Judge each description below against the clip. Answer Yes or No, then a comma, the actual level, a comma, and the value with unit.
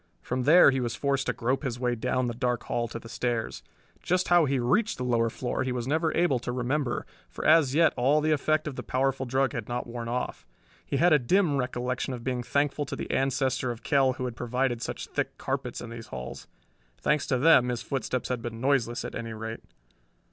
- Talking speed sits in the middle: No, fast, 225 wpm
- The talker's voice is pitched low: Yes, low, 130 Hz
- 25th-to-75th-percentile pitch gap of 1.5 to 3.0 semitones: Yes, narrow, 2.6 semitones